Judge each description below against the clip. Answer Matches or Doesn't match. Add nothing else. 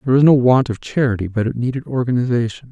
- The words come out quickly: Matches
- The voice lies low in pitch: Matches